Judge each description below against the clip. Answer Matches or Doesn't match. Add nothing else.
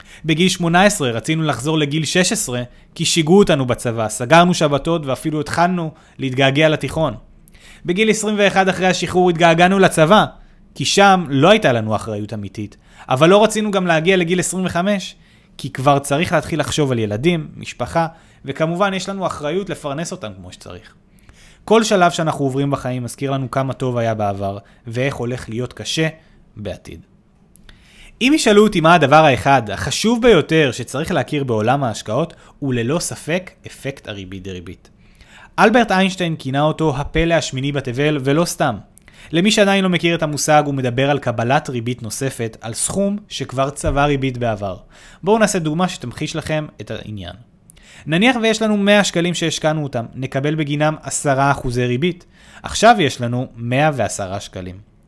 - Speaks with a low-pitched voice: Doesn't match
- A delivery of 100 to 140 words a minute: Doesn't match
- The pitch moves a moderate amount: Doesn't match